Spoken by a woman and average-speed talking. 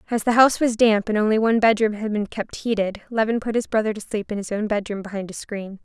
No: female; fast, 265 wpm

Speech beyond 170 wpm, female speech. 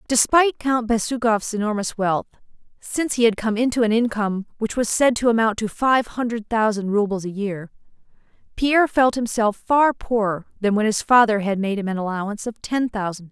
Yes: average, 190 wpm; female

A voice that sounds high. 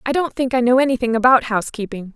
Yes: high, 245 Hz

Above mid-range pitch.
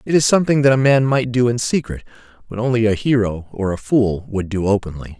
No: low, 115 Hz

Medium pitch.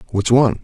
No: low, 120 Hz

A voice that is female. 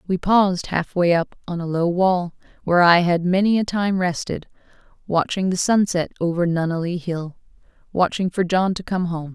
Yes: female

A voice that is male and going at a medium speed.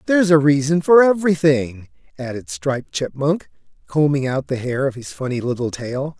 Yes: male; average, 165 wpm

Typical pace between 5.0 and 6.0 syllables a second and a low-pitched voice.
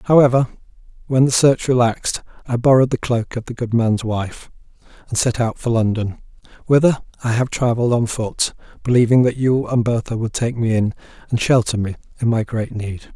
Yes: 5.6 syllables/s; low, 120 Hz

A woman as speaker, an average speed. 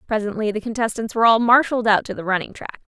No: female; fast, 225 wpm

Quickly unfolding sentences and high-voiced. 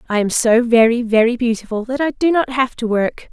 Yes: fast, 235 wpm; high, 240 Hz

